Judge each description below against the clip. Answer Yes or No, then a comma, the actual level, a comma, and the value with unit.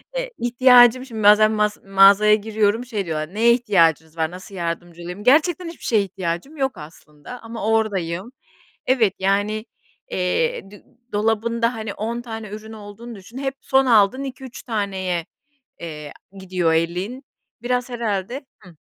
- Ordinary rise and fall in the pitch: Yes, average, 4.4 semitones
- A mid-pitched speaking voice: No, high, 215 Hz